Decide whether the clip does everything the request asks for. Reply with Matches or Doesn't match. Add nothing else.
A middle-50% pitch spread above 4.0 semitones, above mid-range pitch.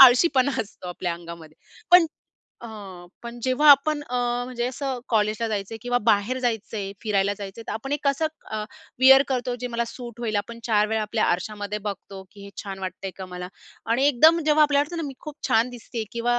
Matches